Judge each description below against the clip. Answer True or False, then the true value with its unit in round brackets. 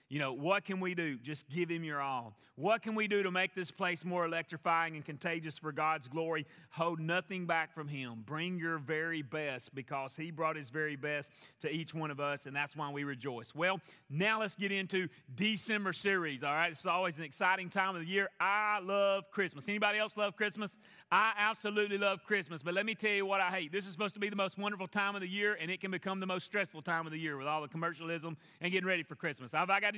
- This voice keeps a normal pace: False (240 wpm)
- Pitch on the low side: False (175 Hz)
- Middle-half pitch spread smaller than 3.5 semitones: False (4.1 semitones)